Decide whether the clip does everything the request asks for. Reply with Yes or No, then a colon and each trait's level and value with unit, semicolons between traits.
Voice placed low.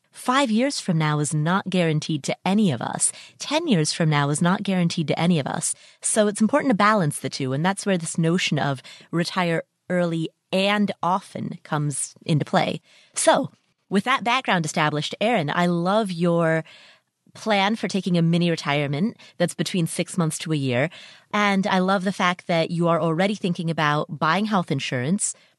No: medium, 175 Hz